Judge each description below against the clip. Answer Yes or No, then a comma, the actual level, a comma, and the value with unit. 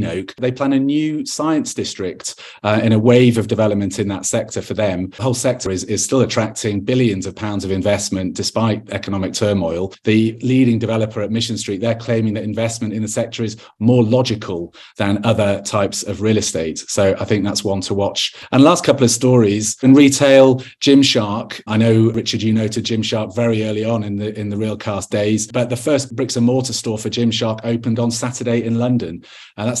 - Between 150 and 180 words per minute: No, fast, 205 wpm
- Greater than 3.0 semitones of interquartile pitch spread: No, narrow, 2.5 semitones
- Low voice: Yes, low, 110 Hz